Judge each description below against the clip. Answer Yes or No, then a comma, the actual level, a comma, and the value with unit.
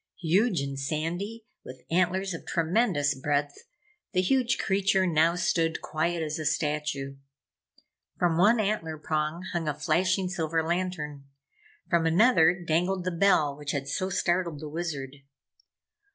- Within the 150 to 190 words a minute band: No, average, 140 wpm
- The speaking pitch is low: No, medium, 165 Hz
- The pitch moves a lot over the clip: No, average, 3.4 semitones